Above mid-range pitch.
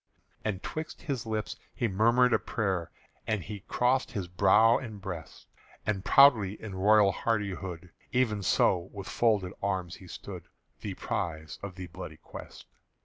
No: low, 100 Hz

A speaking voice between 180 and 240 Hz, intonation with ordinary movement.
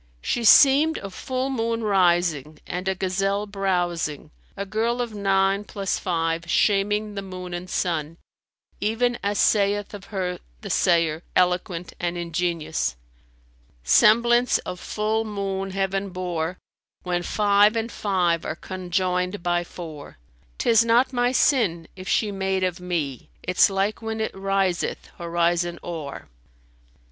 Yes: high, 190 Hz; average, 3.2 semitones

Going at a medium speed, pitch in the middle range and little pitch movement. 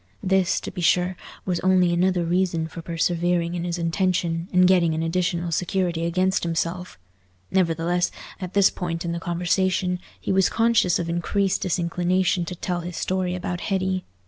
Yes: average, 165 wpm; medium, 180 Hz; narrow, 1.6 semitones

